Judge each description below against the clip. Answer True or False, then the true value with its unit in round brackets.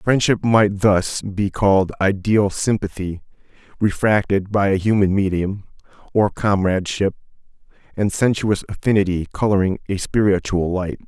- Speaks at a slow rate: True (115 wpm)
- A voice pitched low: True (100 Hz)